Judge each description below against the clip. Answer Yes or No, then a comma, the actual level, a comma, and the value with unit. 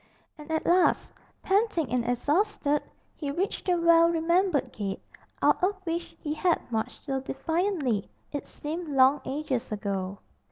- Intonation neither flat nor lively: Yes, average, 5.0 semitones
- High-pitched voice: Yes, very high, 305 Hz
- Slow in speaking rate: No, average, 145 wpm